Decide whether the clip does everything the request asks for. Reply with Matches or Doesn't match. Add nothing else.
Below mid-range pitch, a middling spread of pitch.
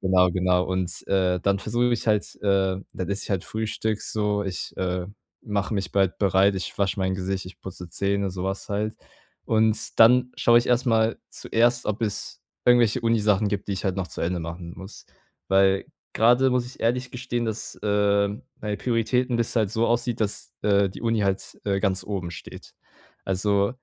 Matches